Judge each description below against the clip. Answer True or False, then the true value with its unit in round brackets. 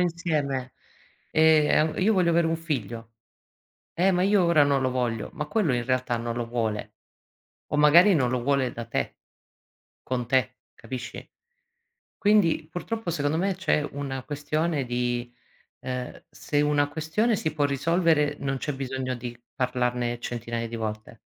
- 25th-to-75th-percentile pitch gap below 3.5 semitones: False (4.8 semitones)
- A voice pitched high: False (140 Hz)